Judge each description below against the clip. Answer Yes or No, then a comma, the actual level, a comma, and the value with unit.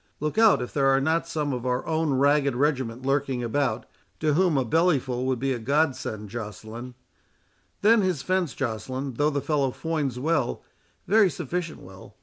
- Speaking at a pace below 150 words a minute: No, average, 175 wpm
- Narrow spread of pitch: No, average, 4.1 semitones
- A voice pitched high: No, medium, 140 Hz